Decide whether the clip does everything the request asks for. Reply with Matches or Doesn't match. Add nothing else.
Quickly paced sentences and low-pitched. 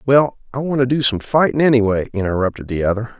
Doesn't match